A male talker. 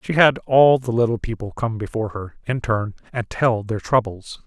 Yes: male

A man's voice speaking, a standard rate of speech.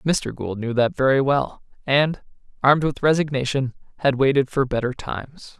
Yes: male; average, 160 wpm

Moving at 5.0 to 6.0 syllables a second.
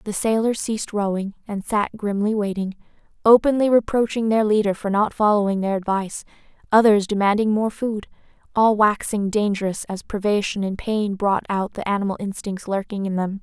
Yes: 5.2 syllables/s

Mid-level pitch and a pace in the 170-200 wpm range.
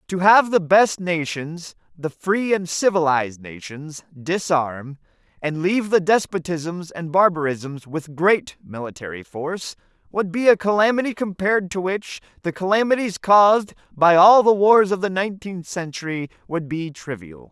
No: medium, 175 Hz; average, 145 wpm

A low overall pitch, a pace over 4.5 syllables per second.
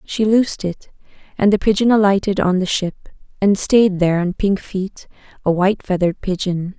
No: high, 195 Hz; 5.3 syllables/s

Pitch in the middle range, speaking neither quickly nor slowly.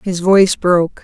Yes: medium, 180 Hz; average, 175 wpm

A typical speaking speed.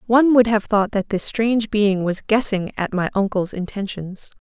Yes: average, 190 wpm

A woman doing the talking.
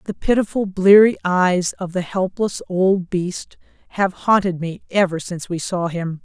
Yes: female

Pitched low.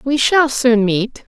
No: very high, 250 Hz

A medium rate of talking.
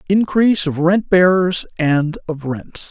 Yes: average, 145 wpm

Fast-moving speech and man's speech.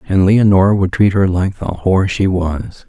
Yes: fast, 210 wpm; male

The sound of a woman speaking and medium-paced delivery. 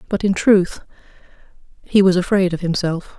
Yes: female; average, 150 wpm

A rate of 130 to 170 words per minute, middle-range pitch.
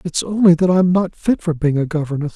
No: fast, 255 wpm; medium, 165 Hz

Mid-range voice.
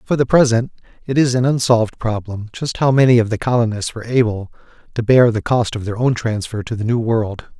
No: low, 115 Hz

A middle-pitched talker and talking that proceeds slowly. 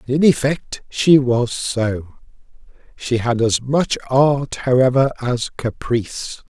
No: low, 125 Hz; slow, 130 wpm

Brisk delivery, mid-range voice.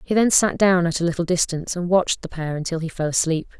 Yes: fast, 265 wpm; medium, 175 Hz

